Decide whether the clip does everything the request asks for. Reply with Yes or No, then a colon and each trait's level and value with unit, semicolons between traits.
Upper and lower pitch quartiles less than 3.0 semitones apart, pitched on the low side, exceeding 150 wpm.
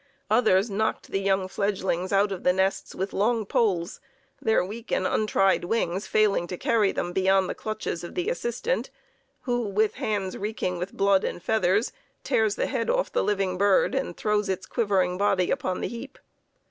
No: narrow, 2.6 semitones; high, 200 Hz; average, 180 wpm